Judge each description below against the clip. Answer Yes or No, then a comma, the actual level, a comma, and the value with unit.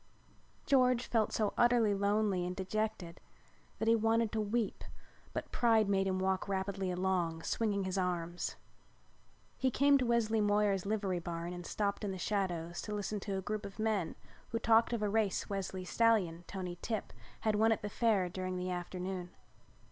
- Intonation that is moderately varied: Yes, average, 3.0 semitones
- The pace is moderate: Yes, average, 175 wpm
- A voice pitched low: No, high, 200 Hz